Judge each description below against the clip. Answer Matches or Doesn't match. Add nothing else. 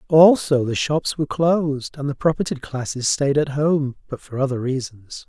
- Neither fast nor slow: Matches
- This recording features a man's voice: Matches